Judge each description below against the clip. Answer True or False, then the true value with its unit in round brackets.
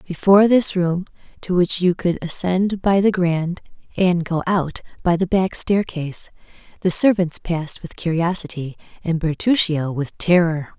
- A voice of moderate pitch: True (175 Hz)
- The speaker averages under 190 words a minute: True (150 wpm)